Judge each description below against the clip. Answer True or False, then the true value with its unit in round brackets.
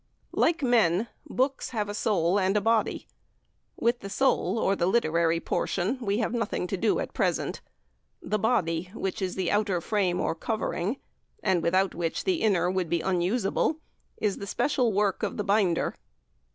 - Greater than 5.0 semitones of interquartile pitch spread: False (4.0 semitones)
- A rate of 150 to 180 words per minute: True (165 wpm)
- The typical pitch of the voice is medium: False (200 Hz)